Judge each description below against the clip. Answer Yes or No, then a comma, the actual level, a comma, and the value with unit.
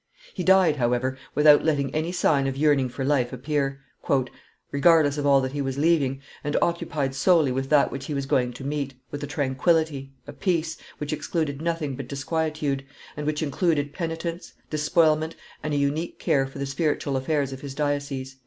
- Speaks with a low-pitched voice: No, medium, 145 Hz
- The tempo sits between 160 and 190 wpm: Yes, average, 180 wpm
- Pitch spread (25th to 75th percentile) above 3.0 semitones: No, narrow, 2.4 semitones